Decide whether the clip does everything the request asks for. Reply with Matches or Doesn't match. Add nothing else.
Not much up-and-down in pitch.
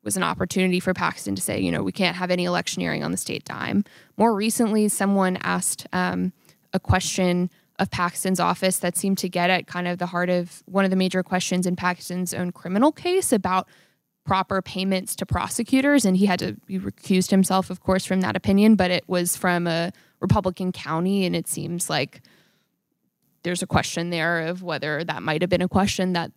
Matches